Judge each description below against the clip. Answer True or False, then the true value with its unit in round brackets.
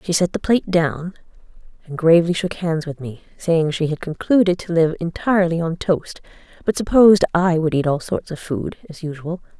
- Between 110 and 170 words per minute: False (195 wpm)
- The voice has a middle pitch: True (170 Hz)